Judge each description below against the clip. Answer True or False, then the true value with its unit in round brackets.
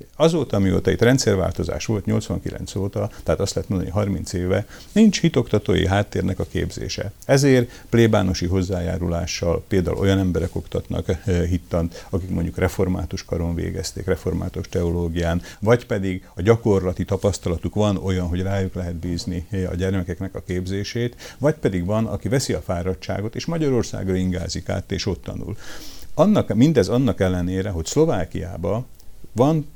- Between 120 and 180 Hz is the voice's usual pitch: False (95 Hz)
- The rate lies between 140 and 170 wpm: True (145 wpm)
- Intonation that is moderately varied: True (3.0 semitones)